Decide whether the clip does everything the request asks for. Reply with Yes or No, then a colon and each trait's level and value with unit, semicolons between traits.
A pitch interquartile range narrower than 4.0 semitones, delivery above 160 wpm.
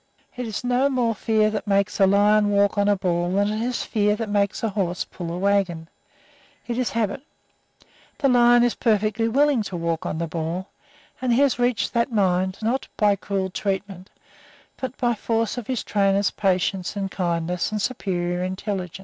Yes: average, 3.6 semitones; average, 185 wpm